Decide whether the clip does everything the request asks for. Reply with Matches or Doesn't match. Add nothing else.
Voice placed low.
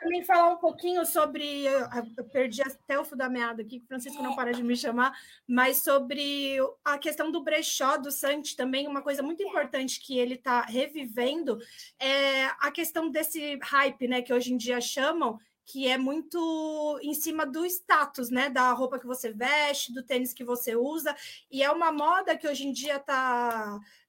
Doesn't match